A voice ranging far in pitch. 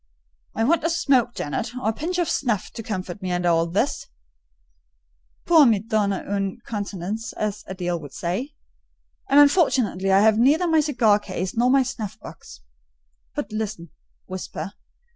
Yes: wide, 5.9 semitones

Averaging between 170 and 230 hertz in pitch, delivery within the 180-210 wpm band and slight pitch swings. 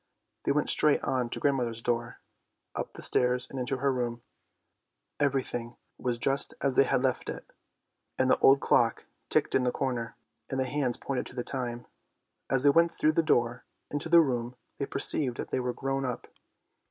No: low, 130 Hz; average, 190 wpm; narrow, 2.2 semitones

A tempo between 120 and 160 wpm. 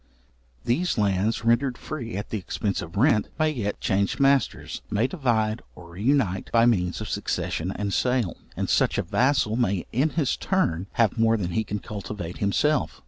No: average, 175 wpm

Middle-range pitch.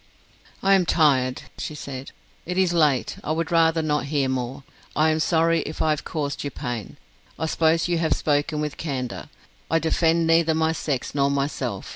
Yes: medium, 155 Hz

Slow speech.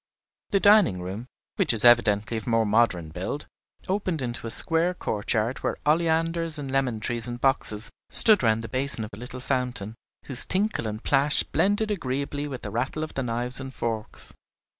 No: average, 180 wpm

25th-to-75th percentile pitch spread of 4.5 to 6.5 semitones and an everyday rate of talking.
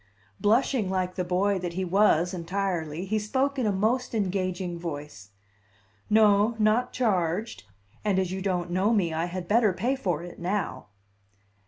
No: average, 3.4 semitones; average, 160 wpm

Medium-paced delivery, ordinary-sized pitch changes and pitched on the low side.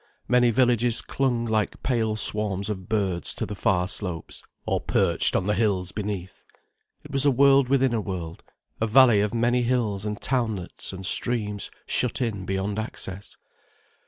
Yes: average, 160 wpm; average, 3.8 semitones; low, 110 Hz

